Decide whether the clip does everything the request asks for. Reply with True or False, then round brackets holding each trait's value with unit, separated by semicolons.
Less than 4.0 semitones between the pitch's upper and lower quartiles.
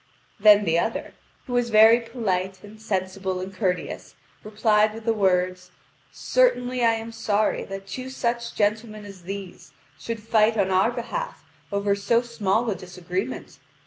True (3.2 semitones)